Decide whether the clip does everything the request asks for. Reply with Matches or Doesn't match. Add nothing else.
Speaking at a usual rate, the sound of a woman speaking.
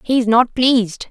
Matches